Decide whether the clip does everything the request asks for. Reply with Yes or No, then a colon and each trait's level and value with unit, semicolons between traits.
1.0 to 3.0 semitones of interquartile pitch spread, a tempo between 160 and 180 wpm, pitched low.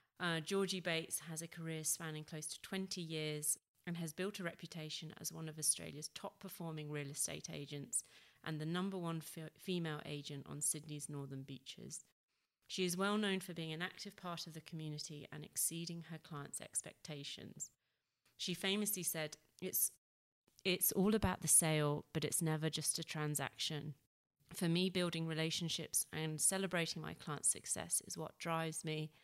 No: narrow, 2.6 semitones; average, 165 wpm; medium, 160 Hz